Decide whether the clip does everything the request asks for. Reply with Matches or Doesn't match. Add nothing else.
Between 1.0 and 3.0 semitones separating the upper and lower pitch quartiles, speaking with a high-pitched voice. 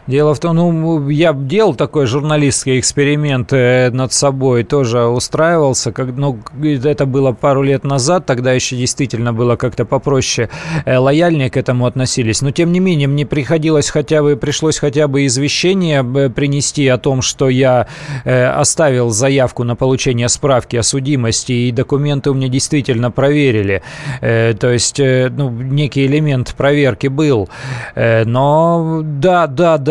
Doesn't match